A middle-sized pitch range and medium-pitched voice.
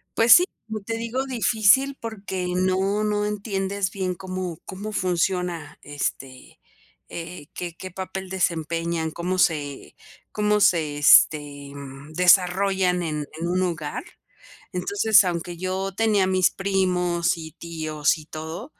Yes: average, 3.3 semitones; medium, 180 Hz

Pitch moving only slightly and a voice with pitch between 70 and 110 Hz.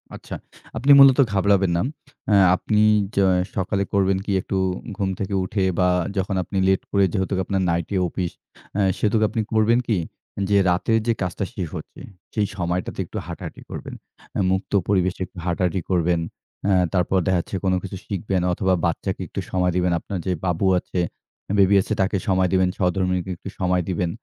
Yes: narrow, 1.7 semitones; very low, 95 Hz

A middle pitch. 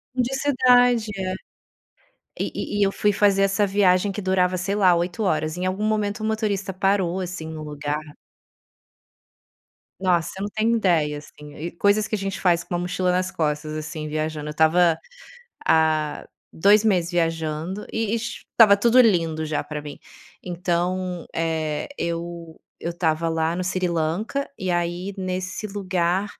Yes: medium, 180 Hz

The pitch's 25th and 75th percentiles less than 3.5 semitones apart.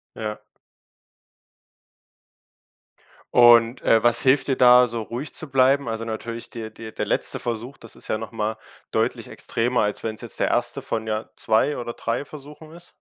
Yes: average, 2.7 semitones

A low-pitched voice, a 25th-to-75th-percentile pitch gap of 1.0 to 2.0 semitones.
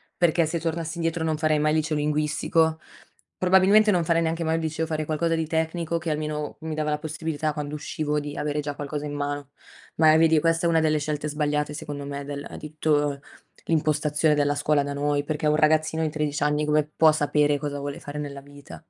No: medium, 150 Hz; narrow, 1.5 semitones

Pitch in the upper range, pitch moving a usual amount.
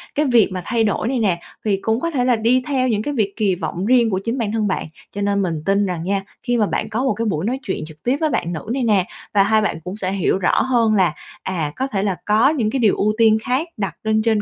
Yes: high, 215 Hz; average, 3.8 semitones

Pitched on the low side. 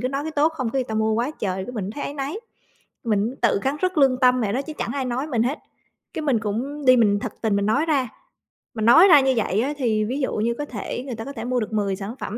No: very high, 250 Hz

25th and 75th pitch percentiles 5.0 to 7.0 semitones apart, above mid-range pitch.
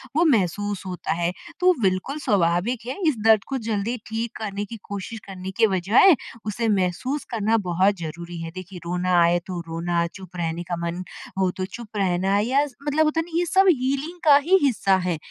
Yes: wide, 5.6 semitones; high, 200 Hz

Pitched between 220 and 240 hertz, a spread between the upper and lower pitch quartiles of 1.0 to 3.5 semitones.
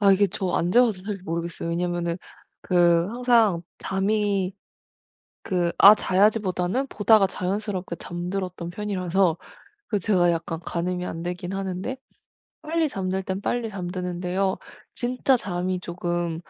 No: medium, 185 Hz; average, 2.8 semitones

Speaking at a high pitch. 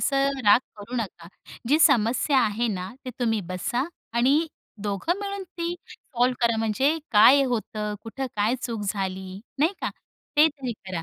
Yes: high, 235 Hz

